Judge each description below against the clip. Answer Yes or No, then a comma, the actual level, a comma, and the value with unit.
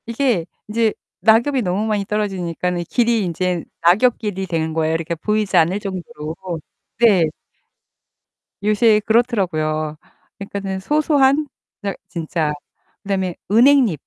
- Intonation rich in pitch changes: No, average, 5.0 semitones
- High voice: Yes, high, 200 Hz